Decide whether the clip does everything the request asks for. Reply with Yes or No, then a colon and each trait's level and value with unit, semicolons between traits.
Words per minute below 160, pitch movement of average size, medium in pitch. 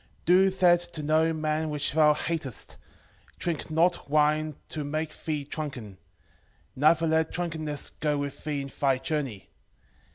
No: average, 150 wpm; narrow, 1.8 semitones; medium, 155 Hz